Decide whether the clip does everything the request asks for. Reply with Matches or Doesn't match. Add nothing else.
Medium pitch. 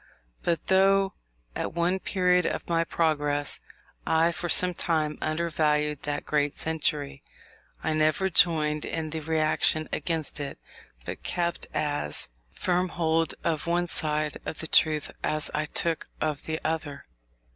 Matches